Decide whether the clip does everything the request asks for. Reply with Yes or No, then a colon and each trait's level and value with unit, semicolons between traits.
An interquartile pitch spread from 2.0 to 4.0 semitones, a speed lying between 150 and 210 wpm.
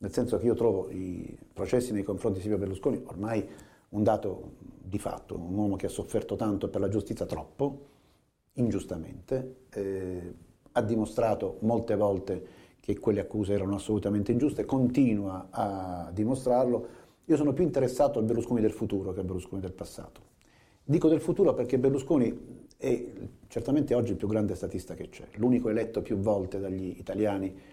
No: average, 4.5 semitones; average, 160 wpm